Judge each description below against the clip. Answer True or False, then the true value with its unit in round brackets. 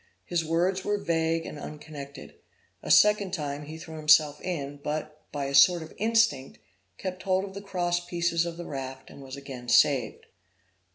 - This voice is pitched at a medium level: True (160 Hz)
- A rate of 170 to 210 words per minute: True (175 wpm)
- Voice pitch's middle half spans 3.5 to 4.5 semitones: True (3.9 semitones)